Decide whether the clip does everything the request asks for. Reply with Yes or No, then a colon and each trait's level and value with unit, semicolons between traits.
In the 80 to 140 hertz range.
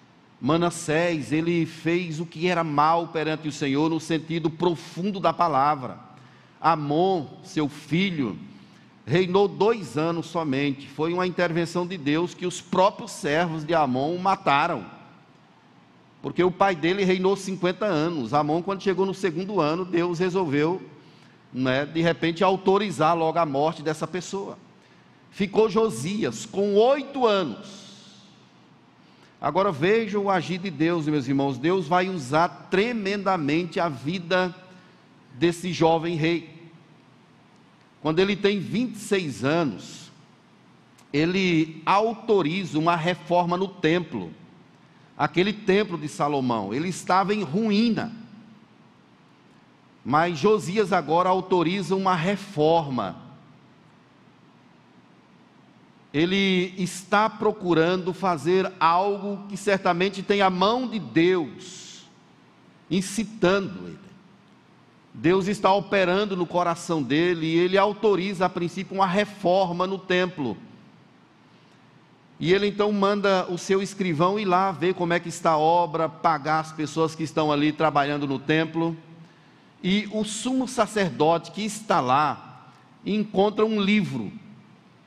No: medium, 180 Hz